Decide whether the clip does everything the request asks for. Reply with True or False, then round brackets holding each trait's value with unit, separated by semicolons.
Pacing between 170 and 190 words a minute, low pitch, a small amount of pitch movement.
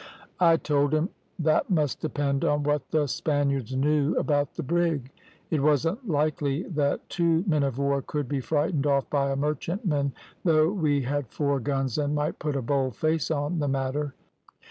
False (175 wpm; 145 Hz; 2.1 semitones)